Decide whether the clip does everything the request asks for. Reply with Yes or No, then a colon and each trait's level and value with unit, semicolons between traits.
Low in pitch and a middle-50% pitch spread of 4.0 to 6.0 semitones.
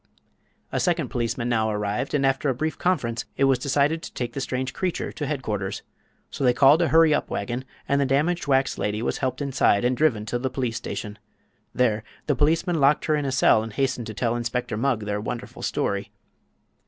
No: low, 130 Hz; average, 3.6 semitones